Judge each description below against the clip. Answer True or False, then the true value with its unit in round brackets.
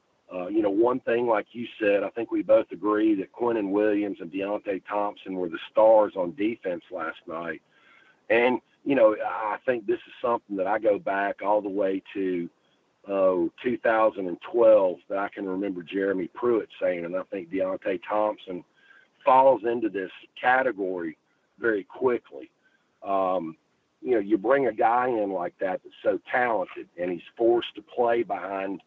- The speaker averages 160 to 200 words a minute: True (170 wpm)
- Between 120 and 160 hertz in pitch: False (105 Hz)